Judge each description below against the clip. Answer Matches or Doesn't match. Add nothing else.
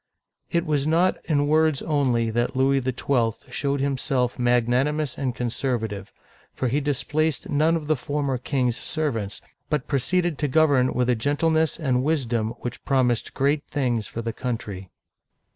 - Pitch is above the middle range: Doesn't match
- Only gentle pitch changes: Doesn't match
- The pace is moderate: Matches